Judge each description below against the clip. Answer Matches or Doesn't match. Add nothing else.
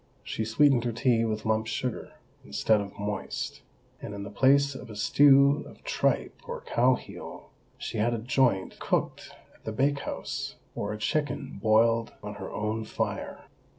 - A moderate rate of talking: Matches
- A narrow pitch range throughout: Doesn't match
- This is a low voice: Matches